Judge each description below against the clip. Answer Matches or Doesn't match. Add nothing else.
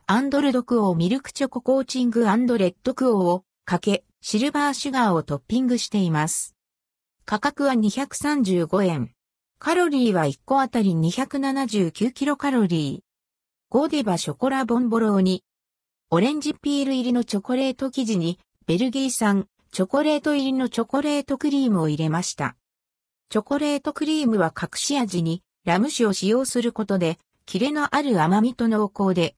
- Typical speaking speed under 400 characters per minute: Matches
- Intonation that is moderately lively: Doesn't match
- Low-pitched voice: Doesn't match